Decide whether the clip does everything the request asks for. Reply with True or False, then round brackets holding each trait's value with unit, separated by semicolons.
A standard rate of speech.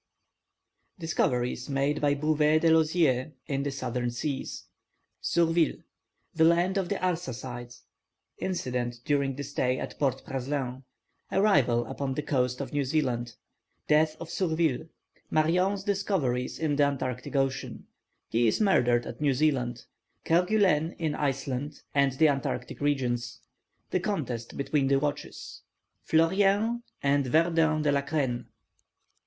False (130 wpm)